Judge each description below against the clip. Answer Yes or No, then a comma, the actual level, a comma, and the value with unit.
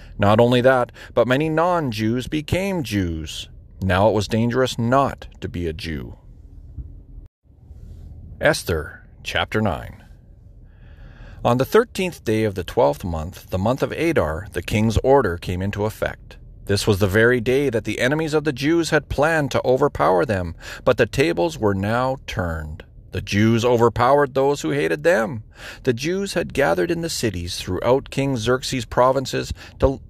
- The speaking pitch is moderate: No, low, 115 Hz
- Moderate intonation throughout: No, wide, 6.0 semitones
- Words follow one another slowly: No, average, 160 wpm